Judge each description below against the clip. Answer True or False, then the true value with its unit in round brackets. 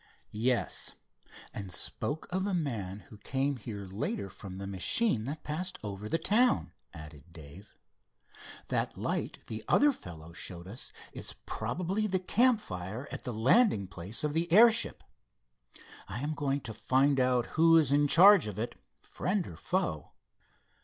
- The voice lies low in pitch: True (130 Hz)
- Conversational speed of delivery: True (155 wpm)